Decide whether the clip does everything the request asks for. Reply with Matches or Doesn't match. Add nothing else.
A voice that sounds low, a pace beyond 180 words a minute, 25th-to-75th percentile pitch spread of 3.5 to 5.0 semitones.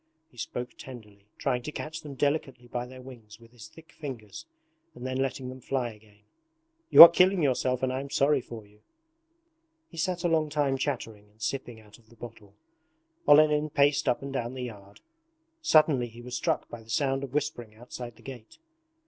Matches